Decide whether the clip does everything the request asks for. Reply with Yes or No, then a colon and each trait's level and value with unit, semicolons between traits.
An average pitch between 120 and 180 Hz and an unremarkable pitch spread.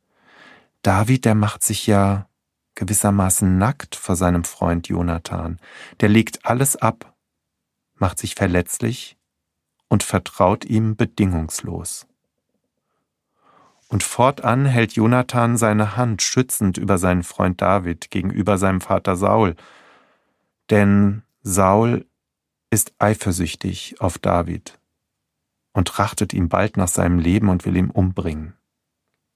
No: low, 100 Hz; average, 3.4 semitones